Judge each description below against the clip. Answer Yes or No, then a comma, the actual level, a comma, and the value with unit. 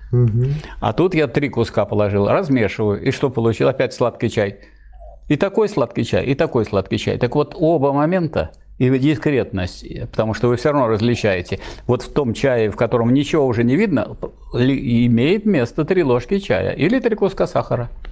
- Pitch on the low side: Yes, low, 125 Hz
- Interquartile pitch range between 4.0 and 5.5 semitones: Yes, average, 4.4 semitones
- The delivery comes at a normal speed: No, fast, 170 wpm